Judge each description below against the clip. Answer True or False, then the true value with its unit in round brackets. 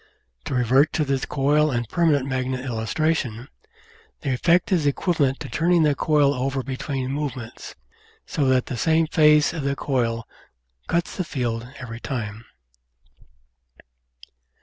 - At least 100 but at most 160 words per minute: True (140 wpm)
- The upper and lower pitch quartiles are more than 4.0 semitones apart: False (3.2 semitones)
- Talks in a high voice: False (135 Hz)